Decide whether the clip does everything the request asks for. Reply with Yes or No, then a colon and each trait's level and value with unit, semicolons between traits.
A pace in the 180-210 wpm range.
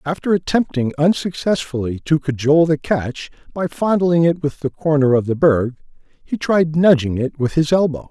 No: average, 170 wpm